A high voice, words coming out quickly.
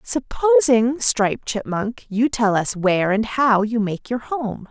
No: high, 220 Hz; average, 165 wpm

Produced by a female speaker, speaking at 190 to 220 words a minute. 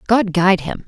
Yes: female; fast, 205 wpm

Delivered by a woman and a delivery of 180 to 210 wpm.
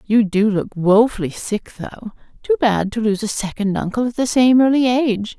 Yes: female; average, 200 wpm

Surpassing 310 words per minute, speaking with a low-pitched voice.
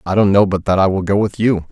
Yes: fast, 350 wpm; low, 100 Hz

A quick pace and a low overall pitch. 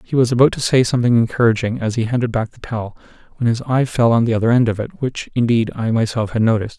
Yes: fast, 255 wpm; low, 115 Hz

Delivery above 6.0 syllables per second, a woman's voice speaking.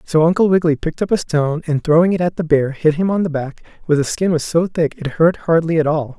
No: 6.4 syllables/s; male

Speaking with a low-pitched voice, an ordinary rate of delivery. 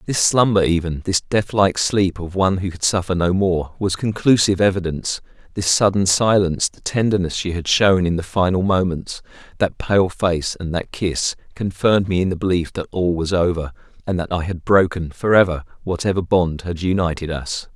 Yes: very low, 90 Hz; average, 180 wpm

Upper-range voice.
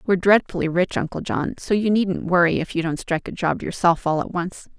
No: medium, 180 Hz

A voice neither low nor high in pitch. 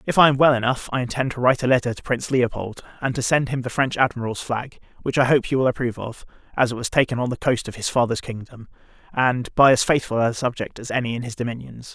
No: low, 125 Hz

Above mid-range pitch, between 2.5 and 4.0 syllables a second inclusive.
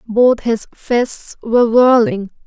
Yes: high, 230 Hz; 3.4 syllables/s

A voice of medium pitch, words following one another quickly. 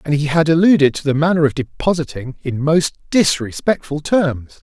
No: medium, 155 Hz; average, 165 wpm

